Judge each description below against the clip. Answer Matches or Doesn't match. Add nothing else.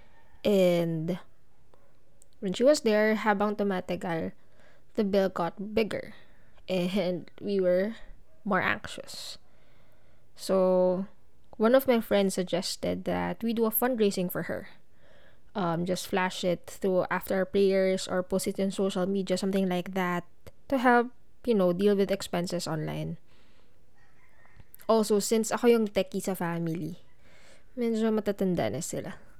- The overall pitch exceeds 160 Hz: Matches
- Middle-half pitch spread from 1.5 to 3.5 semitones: Matches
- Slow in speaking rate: Doesn't match